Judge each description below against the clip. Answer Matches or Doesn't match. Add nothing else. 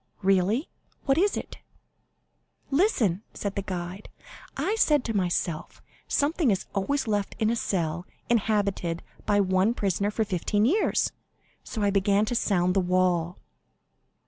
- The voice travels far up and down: Doesn't match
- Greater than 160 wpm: Doesn't match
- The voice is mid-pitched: Doesn't match